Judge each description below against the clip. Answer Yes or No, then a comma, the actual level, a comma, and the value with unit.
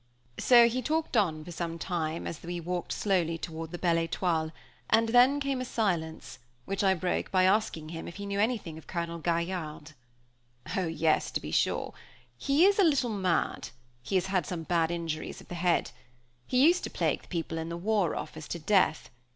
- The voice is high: No, medium, 175 Hz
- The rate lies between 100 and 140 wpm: No, average, 200 wpm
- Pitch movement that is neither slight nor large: Yes, average, 4.4 semitones